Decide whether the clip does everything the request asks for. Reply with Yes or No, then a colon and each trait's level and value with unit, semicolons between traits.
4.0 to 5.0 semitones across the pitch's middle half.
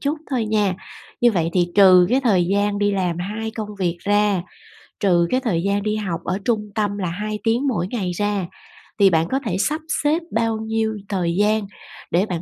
No: average, 3.3 semitones